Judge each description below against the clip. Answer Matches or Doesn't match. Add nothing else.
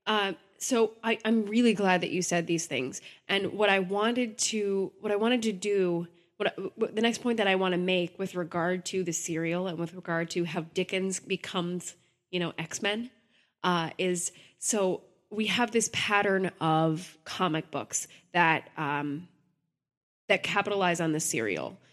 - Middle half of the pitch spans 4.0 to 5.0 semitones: Doesn't match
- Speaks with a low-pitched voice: Doesn't match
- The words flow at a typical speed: Matches